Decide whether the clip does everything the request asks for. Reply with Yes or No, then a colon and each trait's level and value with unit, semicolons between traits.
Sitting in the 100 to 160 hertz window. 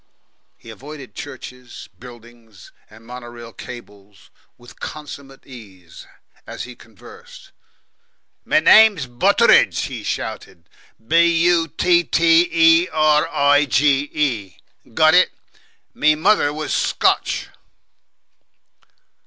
Yes: medium, 140 Hz